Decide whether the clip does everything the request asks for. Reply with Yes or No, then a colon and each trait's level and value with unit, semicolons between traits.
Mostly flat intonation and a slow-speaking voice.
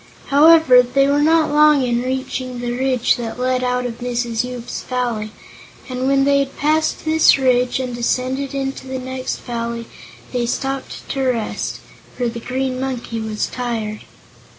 No: narrow, 2.0 semitones; average, 165 wpm